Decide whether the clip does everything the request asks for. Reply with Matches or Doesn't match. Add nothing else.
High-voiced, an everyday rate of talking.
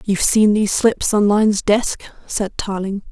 Matches